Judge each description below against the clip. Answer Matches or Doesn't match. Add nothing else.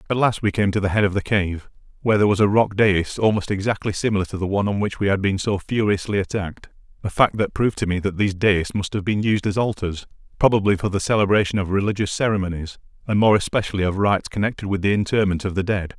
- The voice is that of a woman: Doesn't match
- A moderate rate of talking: Doesn't match